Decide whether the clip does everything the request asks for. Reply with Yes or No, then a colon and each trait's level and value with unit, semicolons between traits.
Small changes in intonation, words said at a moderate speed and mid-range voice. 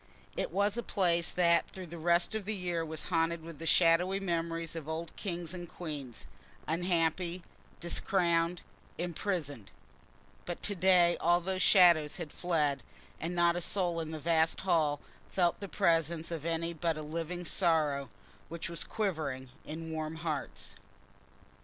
Yes: narrow, 1.7 semitones; average, 155 wpm; medium, 170 Hz